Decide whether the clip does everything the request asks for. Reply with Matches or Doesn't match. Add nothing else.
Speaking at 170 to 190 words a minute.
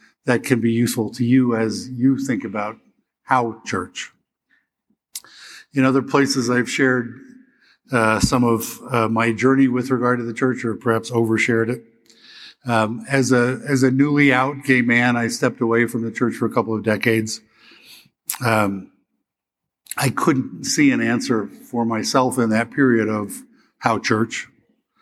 Doesn't match